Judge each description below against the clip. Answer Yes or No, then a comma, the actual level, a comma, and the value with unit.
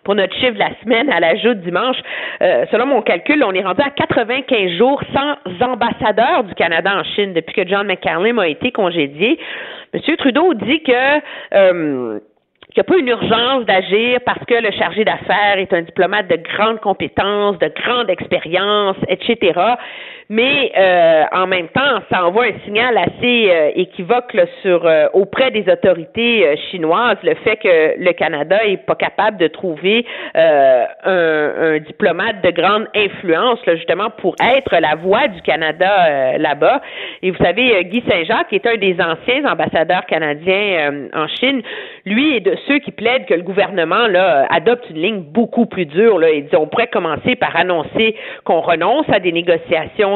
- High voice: Yes, high, 205 Hz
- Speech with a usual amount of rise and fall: No, wide, 5.7 semitones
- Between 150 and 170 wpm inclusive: No, average, 180 wpm